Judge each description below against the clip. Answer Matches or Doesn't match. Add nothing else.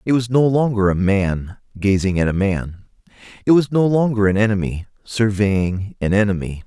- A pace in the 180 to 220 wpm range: Doesn't match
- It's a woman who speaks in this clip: Doesn't match